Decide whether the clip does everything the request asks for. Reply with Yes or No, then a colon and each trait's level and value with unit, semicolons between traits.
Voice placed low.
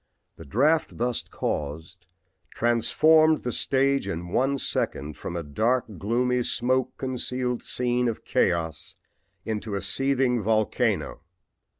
Yes: low, 120 Hz